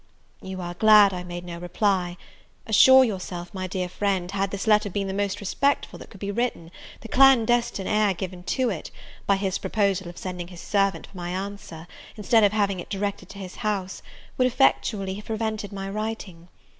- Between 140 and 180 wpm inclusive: No, average, 190 wpm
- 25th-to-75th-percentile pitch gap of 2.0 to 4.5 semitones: Yes, narrow, 2.6 semitones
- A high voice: Yes, high, 195 Hz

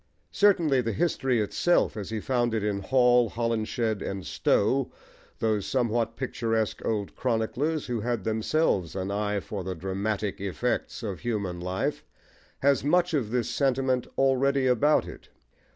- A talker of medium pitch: No, low, 115 Hz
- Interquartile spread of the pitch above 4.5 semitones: No, average, 4.2 semitones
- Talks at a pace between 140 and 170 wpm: Yes, average, 145 wpm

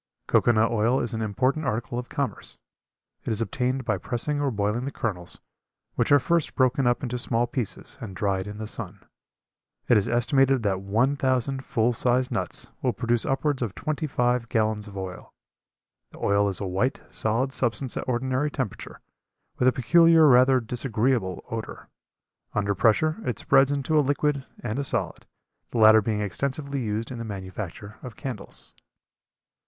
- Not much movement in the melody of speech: No, average, 3.8 semitones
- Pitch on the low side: Yes, low, 120 Hz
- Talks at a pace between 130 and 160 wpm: No, average, 170 wpm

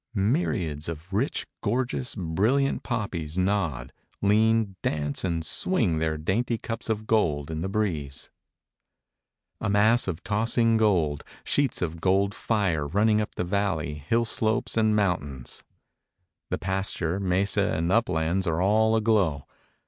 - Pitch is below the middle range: Yes, very low, 95 Hz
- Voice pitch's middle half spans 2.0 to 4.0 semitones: No, average, 5.3 semitones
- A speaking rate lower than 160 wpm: Yes, slow, 135 wpm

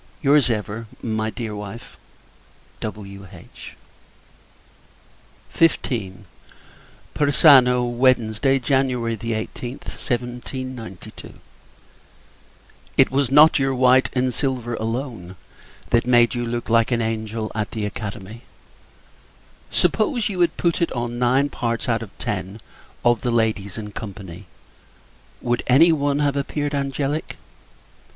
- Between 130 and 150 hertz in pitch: No, low, 120 Hz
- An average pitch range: Yes, average, 3.4 semitones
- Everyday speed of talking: No, slow, 110 wpm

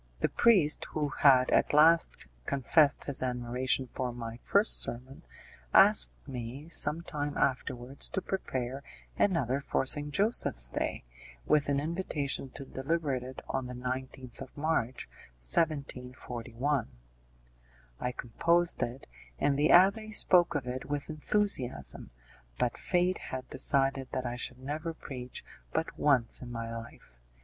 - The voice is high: No, low, 135 Hz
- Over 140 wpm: No, slow, 135 wpm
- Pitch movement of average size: Yes, average, 3.6 semitones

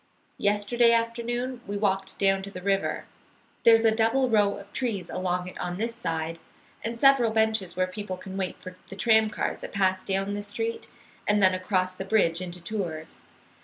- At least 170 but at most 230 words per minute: Yes, average, 185 wpm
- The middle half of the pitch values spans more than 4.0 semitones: No, average, 3.4 semitones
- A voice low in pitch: No, high, 200 Hz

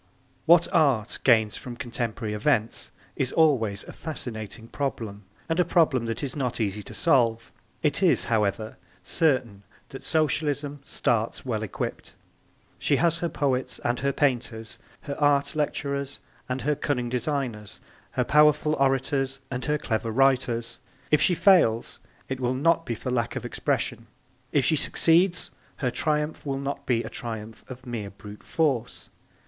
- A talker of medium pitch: No, low, 130 Hz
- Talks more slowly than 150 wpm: No, average, 155 wpm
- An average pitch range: Yes, average, 4.3 semitones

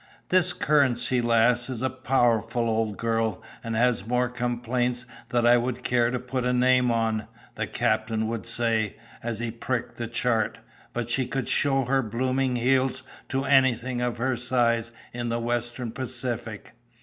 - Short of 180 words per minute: Yes, average, 160 wpm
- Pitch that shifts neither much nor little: No, narrow, 1.7 semitones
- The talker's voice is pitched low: Yes, low, 120 Hz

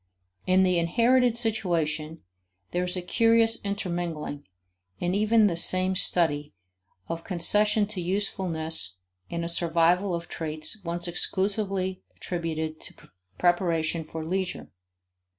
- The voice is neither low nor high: Yes, medium, 175 Hz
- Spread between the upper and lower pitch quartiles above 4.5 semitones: No, average, 3.3 semitones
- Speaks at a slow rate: Yes, slow, 115 wpm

